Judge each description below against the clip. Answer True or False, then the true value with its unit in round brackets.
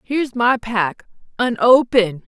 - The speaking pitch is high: True (230 Hz)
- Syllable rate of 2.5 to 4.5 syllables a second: True (4.4 syllables/s)